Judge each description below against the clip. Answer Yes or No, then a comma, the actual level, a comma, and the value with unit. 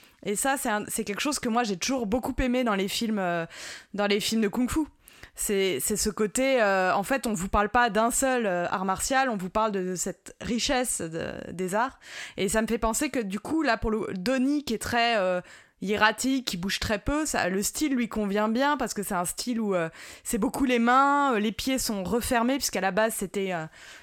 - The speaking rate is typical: No, fast, 240 wpm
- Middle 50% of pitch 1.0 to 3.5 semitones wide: No, average, 4.3 semitones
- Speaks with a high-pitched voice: Yes, high, 225 Hz